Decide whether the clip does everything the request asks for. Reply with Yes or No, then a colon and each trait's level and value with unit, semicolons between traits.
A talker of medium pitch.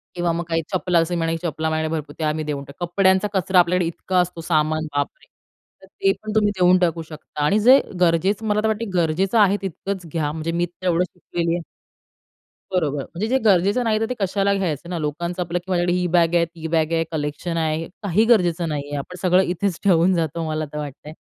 Yes: medium, 175 Hz